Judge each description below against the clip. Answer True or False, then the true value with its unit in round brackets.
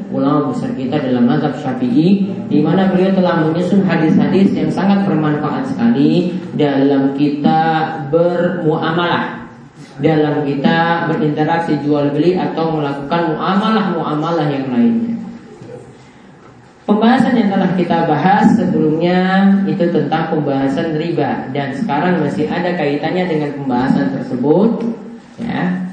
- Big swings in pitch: False (4.4 semitones)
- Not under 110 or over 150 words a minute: True (115 wpm)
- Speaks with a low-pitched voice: False (165 Hz)